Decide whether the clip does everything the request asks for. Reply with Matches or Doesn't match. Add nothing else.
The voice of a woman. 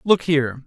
Doesn't match